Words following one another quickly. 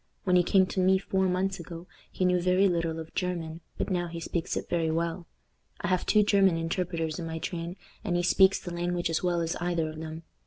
Yes: fast, 230 wpm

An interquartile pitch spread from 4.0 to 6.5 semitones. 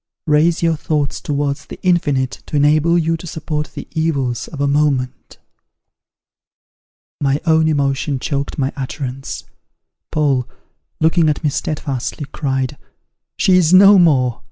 No: average, 2.7 semitones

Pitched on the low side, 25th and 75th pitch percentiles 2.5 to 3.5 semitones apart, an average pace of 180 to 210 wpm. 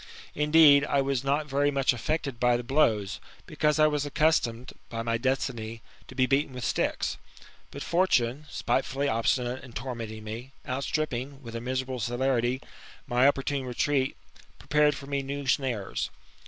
No: low, 130 Hz; average, 2.9 semitones; average, 155 wpm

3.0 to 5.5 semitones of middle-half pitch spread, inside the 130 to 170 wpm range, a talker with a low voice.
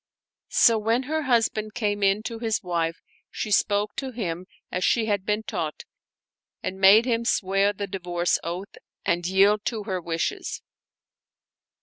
No: average, 3.3 semitones; average, 150 wpm; high, 205 Hz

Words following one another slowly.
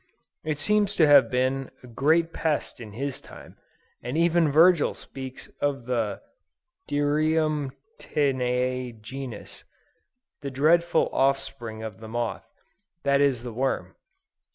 Yes: slow, 125 wpm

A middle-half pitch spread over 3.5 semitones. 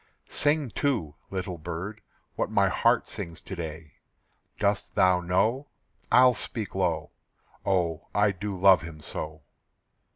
Yes: average, 4.2 semitones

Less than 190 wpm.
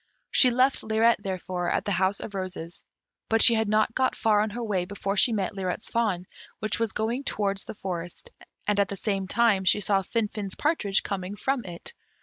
No: average, 200 wpm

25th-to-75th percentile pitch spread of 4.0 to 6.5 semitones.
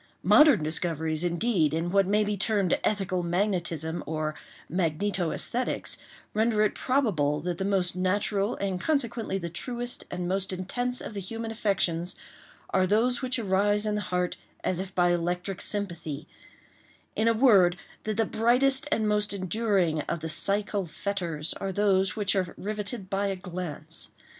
No: average, 3.4 semitones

